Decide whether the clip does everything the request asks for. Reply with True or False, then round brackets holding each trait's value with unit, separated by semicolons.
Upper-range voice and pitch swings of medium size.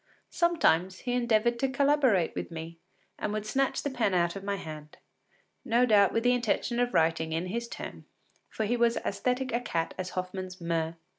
False (210 Hz; 6.0 semitones)